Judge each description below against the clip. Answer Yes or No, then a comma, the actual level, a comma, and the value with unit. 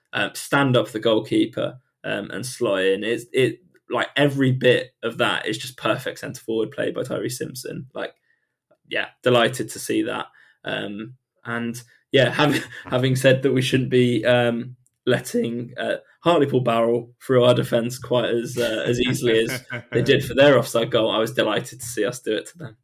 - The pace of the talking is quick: No, average, 185 wpm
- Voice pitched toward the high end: No, low, 120 Hz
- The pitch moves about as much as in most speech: No, narrow, 1.6 semitones